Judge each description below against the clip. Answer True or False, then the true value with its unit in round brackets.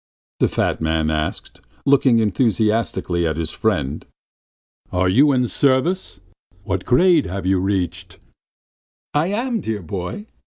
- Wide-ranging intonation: True (7.2 semitones)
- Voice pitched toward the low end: True (105 Hz)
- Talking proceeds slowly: True (130 wpm)